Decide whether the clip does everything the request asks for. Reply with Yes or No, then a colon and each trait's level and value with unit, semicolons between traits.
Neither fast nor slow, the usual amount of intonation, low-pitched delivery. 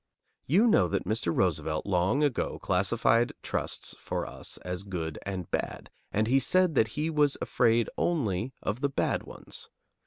No: average, 160 wpm; wide, 7.4 semitones; low, 110 Hz